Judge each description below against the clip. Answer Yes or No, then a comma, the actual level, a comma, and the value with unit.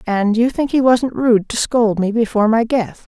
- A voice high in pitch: Yes, high, 230 Hz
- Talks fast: Yes, fast, 230 wpm